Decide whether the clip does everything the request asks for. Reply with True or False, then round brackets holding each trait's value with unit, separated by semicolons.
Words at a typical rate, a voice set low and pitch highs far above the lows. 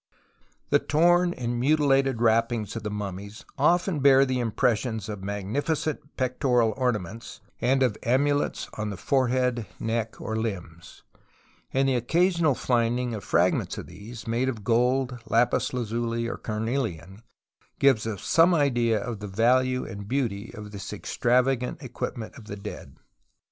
False (145 wpm; 120 Hz; 3.6 semitones)